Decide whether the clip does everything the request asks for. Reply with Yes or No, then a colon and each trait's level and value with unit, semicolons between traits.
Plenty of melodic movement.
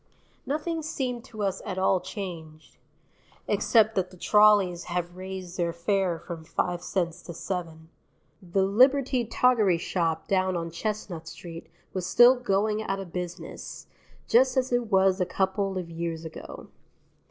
No: average, 3.8 semitones